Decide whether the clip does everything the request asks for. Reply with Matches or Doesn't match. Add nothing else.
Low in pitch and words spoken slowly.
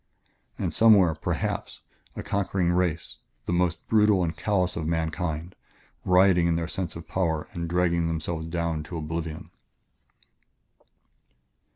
Matches